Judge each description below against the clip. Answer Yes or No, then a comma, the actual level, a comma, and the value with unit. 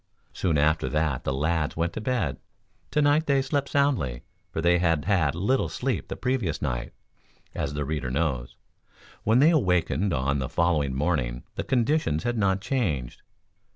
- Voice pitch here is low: Yes, very low, 85 Hz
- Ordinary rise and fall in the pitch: No, wide, 9.0 semitones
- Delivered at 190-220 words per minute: No, average, 160 wpm